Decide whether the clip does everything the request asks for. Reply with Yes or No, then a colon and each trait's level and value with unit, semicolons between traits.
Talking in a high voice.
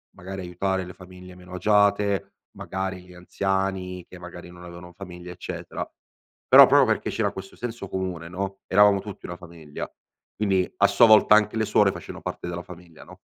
No: very low, 95 Hz